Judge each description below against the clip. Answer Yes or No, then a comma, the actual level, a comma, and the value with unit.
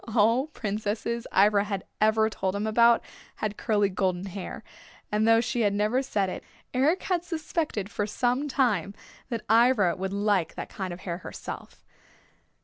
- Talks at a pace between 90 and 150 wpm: No, average, 160 wpm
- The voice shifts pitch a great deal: No, average, 3.0 semitones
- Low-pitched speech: No, high, 215 Hz